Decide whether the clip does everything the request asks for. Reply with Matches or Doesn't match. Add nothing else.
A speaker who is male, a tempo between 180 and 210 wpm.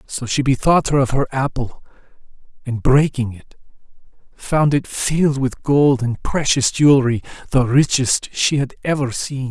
Doesn't match